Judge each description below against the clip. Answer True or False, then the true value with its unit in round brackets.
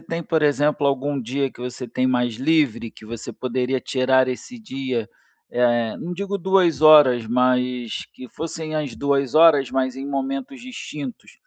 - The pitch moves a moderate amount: True (3.4 semitones)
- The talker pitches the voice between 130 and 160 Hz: True (135 Hz)